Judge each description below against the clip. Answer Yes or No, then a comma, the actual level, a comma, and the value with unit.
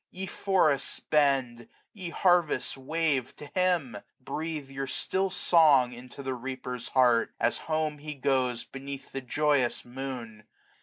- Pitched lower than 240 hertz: Yes, low, 135 Hz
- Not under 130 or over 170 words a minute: Yes, average, 140 wpm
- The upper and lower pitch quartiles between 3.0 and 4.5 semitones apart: Yes, average, 3.7 semitones